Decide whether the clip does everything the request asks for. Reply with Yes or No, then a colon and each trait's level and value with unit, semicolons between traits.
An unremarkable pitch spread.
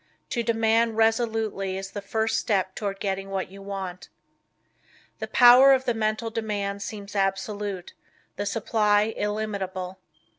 No: narrow, 2.3 semitones